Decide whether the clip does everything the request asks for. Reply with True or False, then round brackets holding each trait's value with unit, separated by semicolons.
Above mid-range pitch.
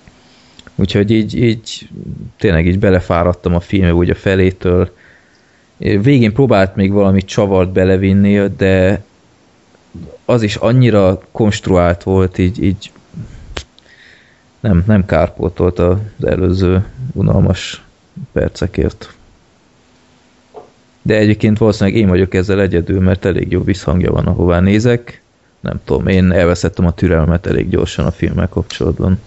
False (95 Hz)